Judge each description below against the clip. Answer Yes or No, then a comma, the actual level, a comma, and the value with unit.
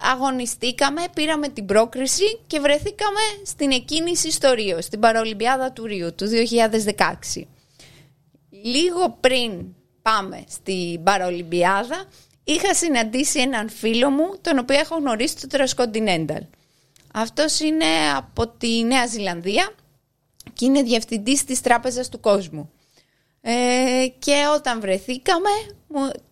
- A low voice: No, high, 245 Hz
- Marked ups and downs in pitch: Yes, wide, 7.0 semitones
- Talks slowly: Yes, slow, 110 wpm